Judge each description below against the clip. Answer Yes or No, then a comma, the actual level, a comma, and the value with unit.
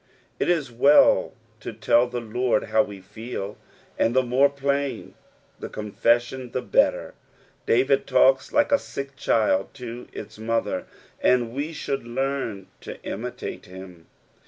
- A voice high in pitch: No, low, 125 Hz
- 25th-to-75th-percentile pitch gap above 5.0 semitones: No, average, 3.6 semitones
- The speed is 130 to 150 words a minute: Yes, average, 140 wpm